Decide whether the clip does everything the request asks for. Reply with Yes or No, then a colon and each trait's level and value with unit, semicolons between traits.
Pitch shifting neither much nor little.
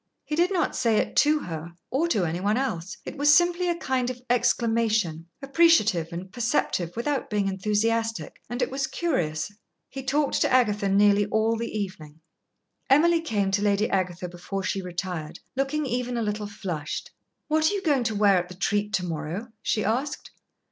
No: wide, 6.1 semitones